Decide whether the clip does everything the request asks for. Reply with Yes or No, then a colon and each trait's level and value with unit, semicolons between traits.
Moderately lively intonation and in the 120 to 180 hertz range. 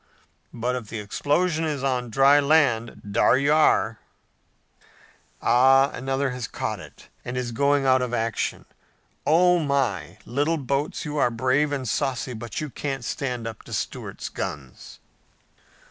Yes: average, 3.3 semitones; low, 135 Hz